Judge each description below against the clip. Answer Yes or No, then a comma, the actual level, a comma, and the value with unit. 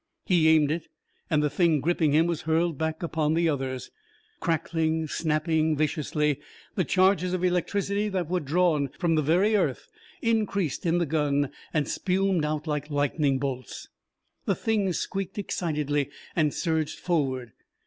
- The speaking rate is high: No, average, 150 wpm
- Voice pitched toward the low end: No, medium, 160 Hz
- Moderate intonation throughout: Yes, average, 3.1 semitones